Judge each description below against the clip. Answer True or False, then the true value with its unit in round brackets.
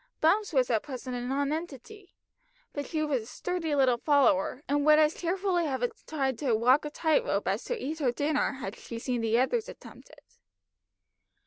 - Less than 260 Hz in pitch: False (285 Hz)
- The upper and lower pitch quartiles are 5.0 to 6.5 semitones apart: False (4.0 semitones)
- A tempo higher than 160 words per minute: True (190 wpm)